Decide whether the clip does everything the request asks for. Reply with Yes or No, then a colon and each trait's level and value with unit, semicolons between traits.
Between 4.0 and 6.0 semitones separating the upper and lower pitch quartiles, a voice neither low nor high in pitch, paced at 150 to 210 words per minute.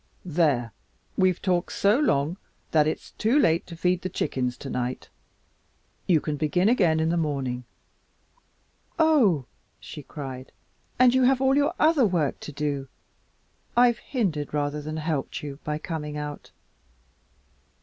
No: wide, 5.4 semitones; medium, 160 Hz; average, 140 wpm